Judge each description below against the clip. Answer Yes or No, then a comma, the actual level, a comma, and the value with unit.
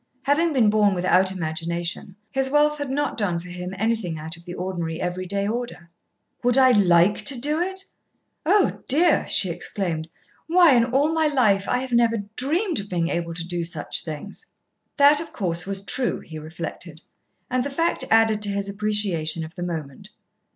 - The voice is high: Yes, high, 200 Hz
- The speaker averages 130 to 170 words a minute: No, average, 185 wpm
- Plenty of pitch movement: Yes, wide, 7.3 semitones